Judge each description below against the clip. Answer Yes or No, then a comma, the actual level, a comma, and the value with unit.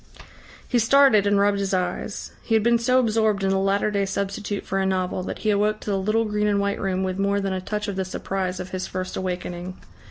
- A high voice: Yes, high, 200 Hz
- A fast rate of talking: Yes, fast, 245 wpm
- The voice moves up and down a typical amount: No, narrow, 2.0 semitones